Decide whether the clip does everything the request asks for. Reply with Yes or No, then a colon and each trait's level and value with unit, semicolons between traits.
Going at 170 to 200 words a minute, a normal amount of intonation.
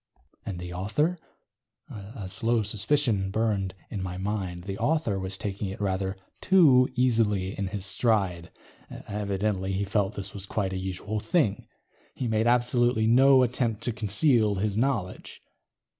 No: average, 145 wpm; average, 3.6 semitones